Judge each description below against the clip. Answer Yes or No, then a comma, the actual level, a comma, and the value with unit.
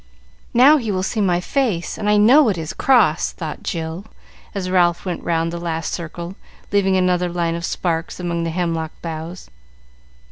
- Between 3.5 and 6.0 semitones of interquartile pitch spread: No, average, 2.9 semitones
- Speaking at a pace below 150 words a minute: No, average, 175 wpm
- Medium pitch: Yes, medium, 175 Hz